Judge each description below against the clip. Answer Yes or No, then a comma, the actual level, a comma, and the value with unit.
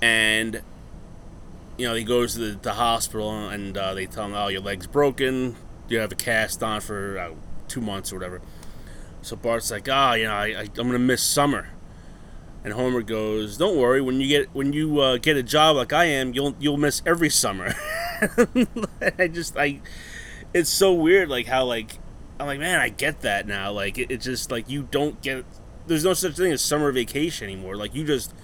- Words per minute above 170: Yes, average, 200 wpm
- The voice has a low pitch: Yes, low, 120 Hz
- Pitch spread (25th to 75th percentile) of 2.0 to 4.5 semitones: No, wide, 5.6 semitones